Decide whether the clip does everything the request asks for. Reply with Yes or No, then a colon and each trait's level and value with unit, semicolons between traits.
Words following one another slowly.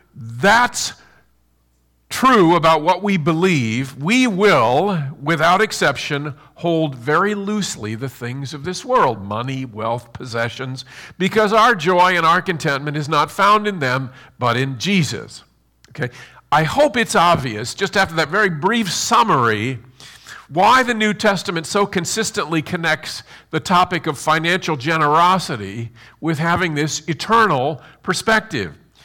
Yes: slow, 130 wpm